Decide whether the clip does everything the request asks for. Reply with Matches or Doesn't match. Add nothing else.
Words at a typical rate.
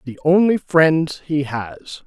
Matches